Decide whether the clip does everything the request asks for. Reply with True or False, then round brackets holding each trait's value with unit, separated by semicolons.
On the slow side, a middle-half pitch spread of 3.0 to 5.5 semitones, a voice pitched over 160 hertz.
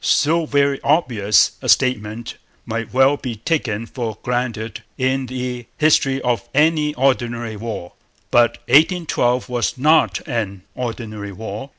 False (125 wpm; 3.4 semitones; 125 Hz)